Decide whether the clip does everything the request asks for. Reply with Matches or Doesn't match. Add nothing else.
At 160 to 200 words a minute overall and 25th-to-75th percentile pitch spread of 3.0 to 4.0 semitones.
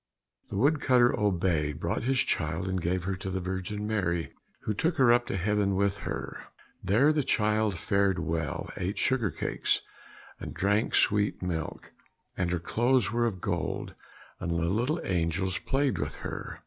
Doesn't match